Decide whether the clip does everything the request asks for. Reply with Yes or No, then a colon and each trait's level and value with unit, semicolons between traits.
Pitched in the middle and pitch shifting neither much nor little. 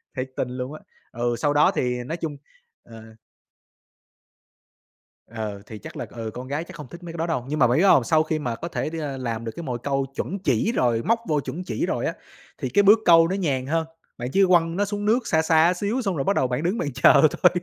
No: medium, 150 Hz; wide, 5.7 semitones